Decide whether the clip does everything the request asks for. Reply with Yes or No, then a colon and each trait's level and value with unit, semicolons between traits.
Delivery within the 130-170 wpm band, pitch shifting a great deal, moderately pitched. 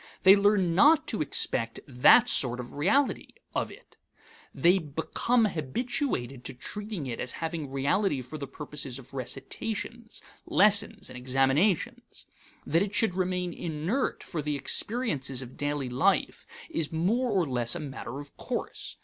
Yes: average, 150 wpm; wide, 7.1 semitones; medium, 155 Hz